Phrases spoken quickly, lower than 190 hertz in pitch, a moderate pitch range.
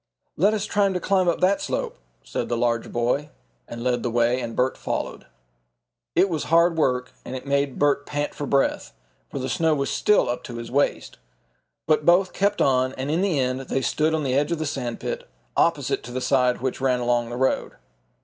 Yes: fast, 215 wpm; low, 135 Hz; average, 4.4 semitones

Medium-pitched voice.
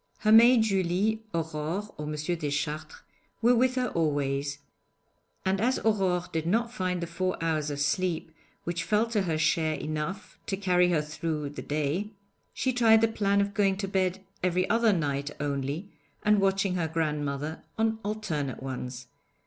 Yes: medium, 180 Hz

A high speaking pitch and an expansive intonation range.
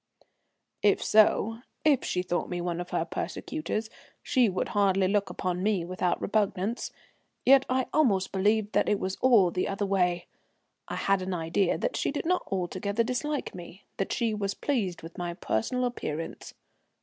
No: high, 195 Hz; average, 4.0 semitones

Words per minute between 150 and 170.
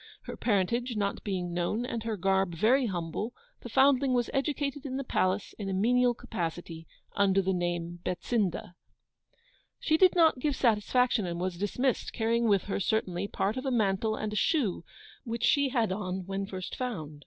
No: average, 180 wpm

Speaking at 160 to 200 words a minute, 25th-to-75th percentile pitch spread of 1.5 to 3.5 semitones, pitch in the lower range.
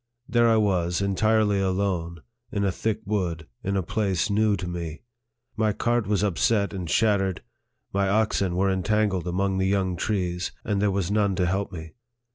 Yes: average, 180 wpm; narrow, 2.5 semitones; low, 100 Hz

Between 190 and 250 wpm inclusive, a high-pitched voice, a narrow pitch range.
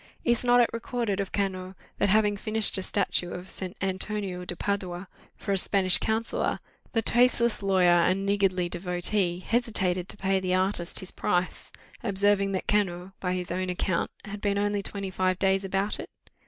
No: average, 175 wpm; high, 195 Hz; narrow, 2.0 semitones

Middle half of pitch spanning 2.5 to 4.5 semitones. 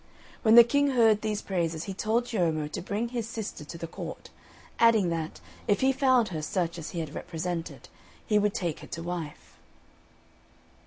No: wide, 5.5 semitones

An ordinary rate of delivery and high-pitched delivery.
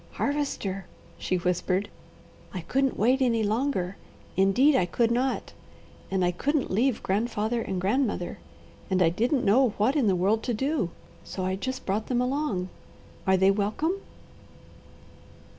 Yes: average, 145 wpm; high, 215 Hz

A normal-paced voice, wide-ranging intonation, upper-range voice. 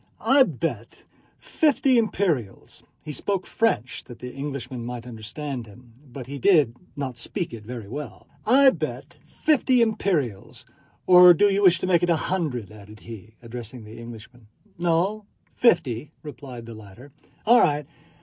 No: average, 145 wpm; wide, 7.8 semitones; medium, 140 Hz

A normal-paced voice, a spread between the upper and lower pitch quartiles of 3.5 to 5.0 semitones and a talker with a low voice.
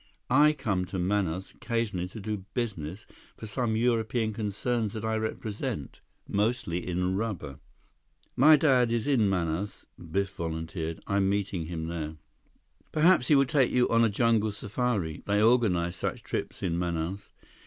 Yes: average, 150 wpm; average, 4.7 semitones; low, 105 Hz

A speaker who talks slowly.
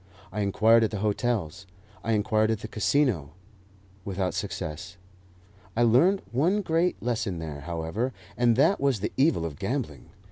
No: average, 150 wpm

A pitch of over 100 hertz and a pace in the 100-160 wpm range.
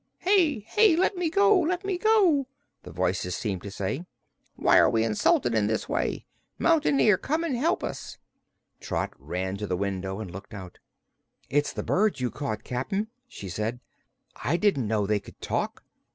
No: low, 135 Hz; average, 175 wpm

